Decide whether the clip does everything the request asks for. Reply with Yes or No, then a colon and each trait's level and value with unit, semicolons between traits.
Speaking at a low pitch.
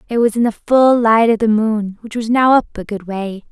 No: high, 225 Hz